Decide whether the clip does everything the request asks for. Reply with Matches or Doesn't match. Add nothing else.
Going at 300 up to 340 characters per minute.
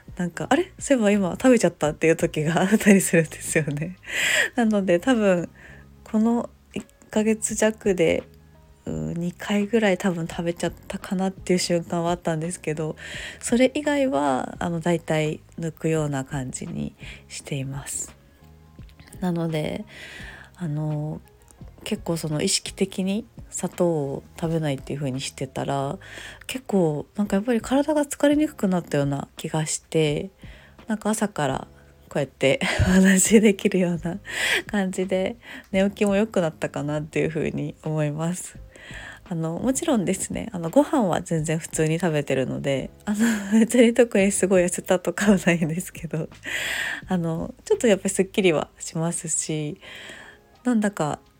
Matches